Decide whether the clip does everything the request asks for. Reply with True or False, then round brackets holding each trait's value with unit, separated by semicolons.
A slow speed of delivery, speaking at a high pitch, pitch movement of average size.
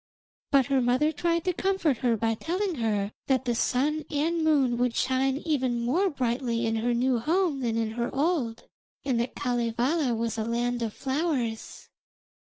False (170 wpm; 255 Hz; 4.4 semitones)